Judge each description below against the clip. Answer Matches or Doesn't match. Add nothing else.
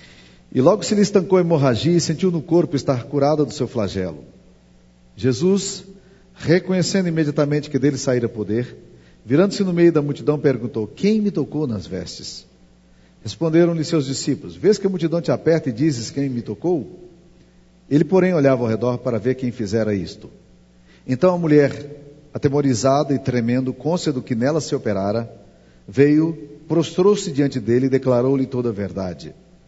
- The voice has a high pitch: Doesn't match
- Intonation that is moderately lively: Doesn't match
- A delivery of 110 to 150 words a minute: Doesn't match